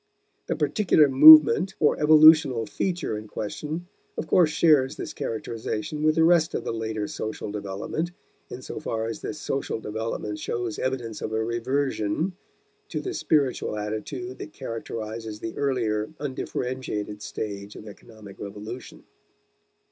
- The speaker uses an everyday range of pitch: No, wide, 5.7 semitones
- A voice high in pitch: No, low, 120 Hz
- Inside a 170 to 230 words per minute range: No, average, 140 wpm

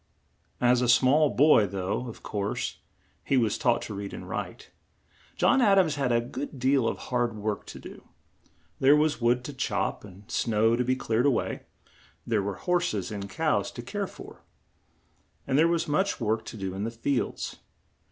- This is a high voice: No, low, 120 Hz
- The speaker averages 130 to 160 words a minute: No, average, 190 wpm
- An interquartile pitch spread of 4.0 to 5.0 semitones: Yes, average, 4.7 semitones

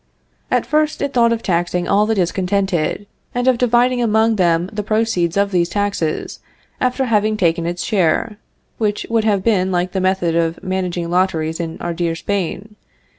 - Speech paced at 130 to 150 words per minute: No, average, 175 wpm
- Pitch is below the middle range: No, high, 190 Hz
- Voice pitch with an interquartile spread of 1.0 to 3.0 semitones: No, average, 4.1 semitones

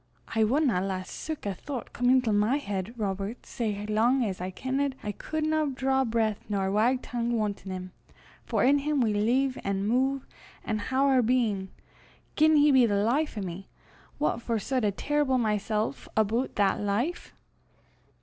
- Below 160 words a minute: No, average, 170 wpm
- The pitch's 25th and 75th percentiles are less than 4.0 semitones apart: No, average, 4.5 semitones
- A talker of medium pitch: No, high, 230 Hz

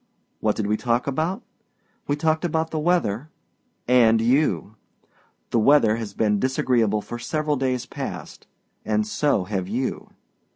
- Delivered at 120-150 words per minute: Yes, average, 140 wpm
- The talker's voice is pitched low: Yes, low, 120 Hz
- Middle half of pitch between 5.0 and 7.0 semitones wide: Yes, wide, 5.6 semitones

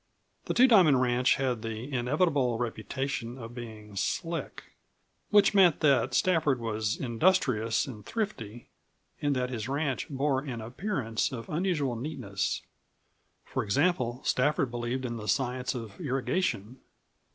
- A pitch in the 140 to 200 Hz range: No, low, 130 Hz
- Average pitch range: Yes, average, 4.3 semitones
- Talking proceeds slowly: Yes, slow, 130 wpm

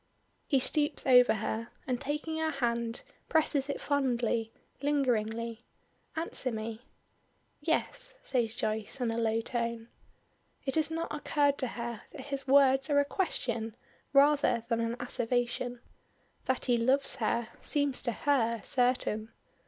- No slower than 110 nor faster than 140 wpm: Yes, slow, 135 wpm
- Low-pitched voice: No, very high, 250 Hz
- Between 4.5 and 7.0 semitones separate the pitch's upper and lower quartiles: No, average, 3.5 semitones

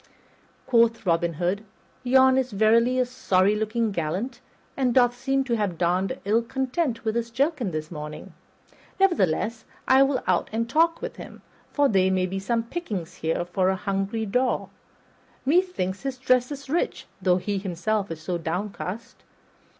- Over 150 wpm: Yes, average, 160 wpm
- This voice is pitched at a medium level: No, high, 220 Hz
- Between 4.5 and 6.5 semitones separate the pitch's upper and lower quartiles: Yes, wide, 5.6 semitones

